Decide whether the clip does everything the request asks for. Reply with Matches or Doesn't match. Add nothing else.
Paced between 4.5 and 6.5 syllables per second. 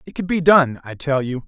Matches